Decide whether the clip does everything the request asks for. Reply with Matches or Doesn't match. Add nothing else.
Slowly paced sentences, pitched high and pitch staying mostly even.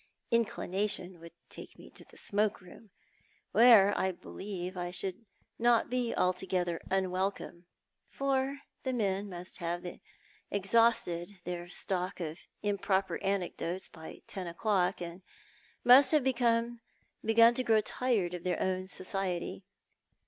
Doesn't match